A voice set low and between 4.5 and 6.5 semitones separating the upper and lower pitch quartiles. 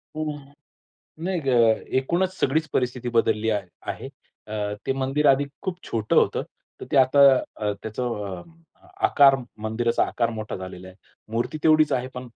Yes: low, 125 Hz; average, 5.0 semitones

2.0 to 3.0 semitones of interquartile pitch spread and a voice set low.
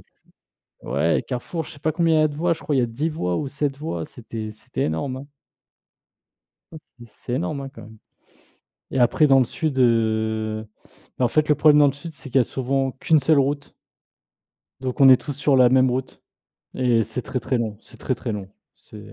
No: average, 4.3 semitones; low, 130 Hz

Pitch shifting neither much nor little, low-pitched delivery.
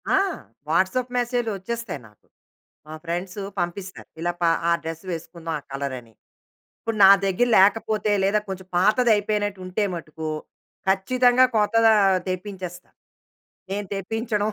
No: average, 4.0 semitones; high, 195 Hz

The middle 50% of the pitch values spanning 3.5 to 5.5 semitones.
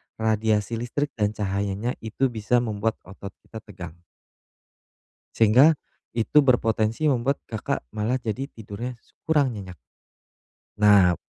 No: average, 3.0 semitones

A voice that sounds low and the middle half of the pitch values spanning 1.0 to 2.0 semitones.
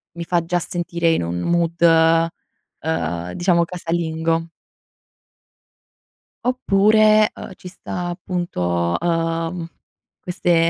No: medium, 170 Hz; narrow, 1.4 semitones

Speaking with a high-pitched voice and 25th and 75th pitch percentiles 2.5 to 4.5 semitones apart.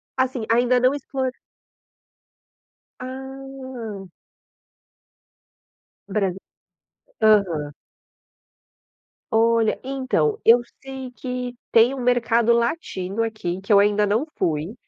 Yes: high, 235 Hz; average, 3.9 semitones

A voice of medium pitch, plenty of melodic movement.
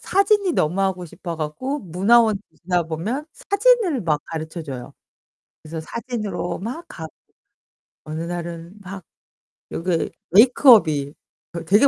Yes: medium, 180 Hz; wide, 6.6 semitones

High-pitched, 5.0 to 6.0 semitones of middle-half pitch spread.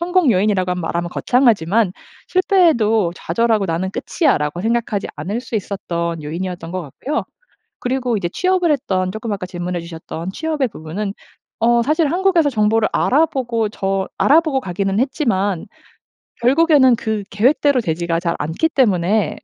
No: high, 215 Hz; wide, 6.7 semitones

